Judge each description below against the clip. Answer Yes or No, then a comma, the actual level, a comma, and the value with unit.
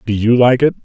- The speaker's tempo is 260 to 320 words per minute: Yes, fast, 285 wpm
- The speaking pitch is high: No, low, 120 Hz